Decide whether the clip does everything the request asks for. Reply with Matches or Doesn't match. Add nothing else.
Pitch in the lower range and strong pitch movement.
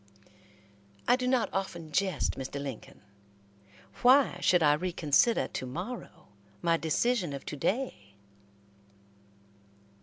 Doesn't match